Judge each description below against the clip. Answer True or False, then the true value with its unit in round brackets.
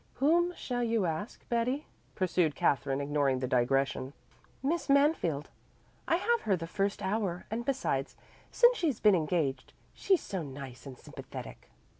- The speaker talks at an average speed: True (145 wpm)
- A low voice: False (185 Hz)